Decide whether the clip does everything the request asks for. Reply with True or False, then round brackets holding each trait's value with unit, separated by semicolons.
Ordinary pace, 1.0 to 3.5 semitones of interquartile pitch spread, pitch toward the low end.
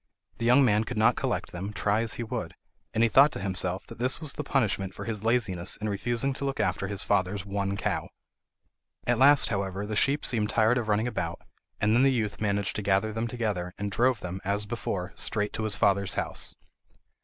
False (215 wpm; 3.1 semitones; 105 Hz)